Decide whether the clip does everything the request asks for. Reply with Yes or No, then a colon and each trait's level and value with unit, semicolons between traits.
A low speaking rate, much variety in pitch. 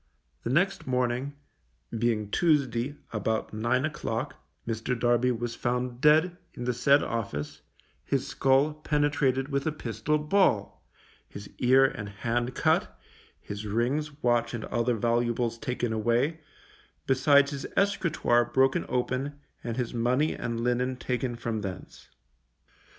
No: slow, 130 wpm; average, 3.3 semitones